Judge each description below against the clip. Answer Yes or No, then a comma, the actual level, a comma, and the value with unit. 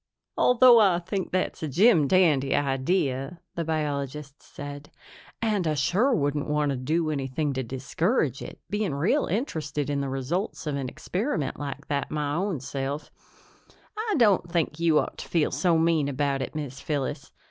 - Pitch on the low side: No, medium, 150 Hz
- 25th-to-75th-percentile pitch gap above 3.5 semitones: Yes, average, 4.3 semitones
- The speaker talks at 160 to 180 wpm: Yes, average, 170 wpm